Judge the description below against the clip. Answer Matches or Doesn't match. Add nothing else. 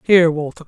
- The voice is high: Doesn't match